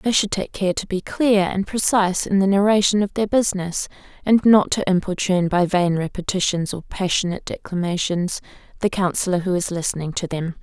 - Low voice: No, high, 190 Hz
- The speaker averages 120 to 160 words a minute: No, average, 180 wpm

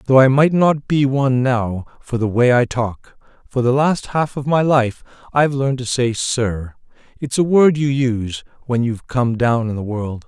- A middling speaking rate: No, fast, 210 wpm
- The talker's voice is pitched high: No, low, 125 Hz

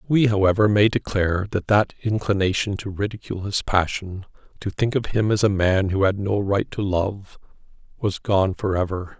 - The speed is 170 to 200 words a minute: Yes, average, 175 wpm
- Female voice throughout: No, male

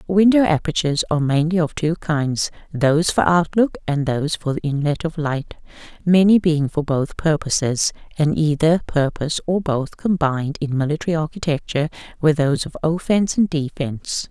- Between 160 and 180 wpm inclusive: No, average, 150 wpm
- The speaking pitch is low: No, medium, 155 Hz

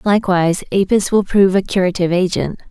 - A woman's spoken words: Yes, female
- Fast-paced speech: No, average, 155 wpm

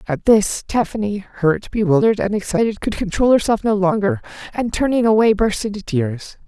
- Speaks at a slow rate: No, average, 165 wpm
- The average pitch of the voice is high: Yes, high, 210 Hz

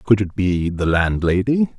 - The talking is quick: No, average, 170 wpm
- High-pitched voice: No, low, 100 Hz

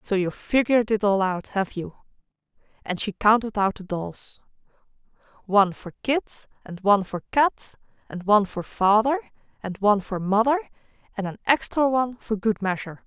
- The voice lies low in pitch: No, high, 215 Hz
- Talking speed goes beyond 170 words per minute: No, average, 160 wpm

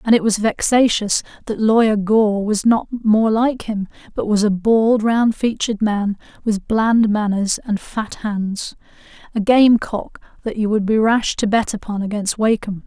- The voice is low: No, high, 215 Hz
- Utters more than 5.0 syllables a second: No, 4.3 syllables/s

